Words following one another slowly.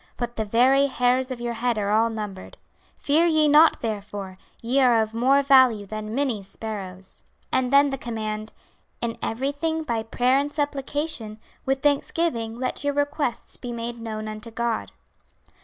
No: average, 160 wpm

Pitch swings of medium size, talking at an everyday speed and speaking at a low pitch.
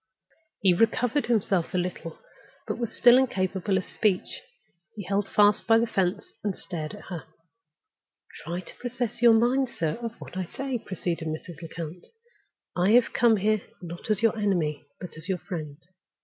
No: average, 4.6 semitones; average, 175 wpm; high, 195 Hz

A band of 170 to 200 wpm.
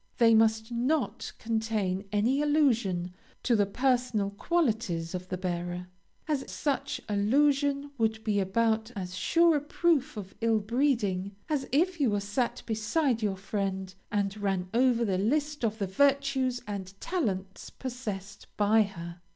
No: average, 145 wpm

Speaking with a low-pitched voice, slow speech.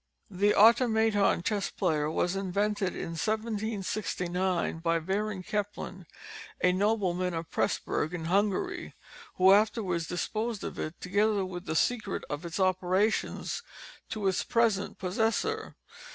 No: high, 195 Hz; slow, 125 wpm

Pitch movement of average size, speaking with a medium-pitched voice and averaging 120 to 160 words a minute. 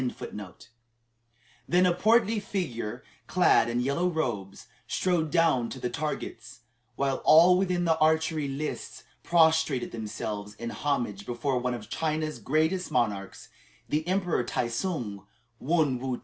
No: wide, 6.0 semitones; medium, 145 Hz; slow, 135 wpm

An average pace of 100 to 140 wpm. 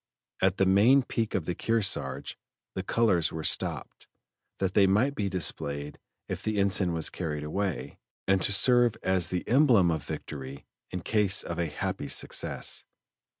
No: average, 160 wpm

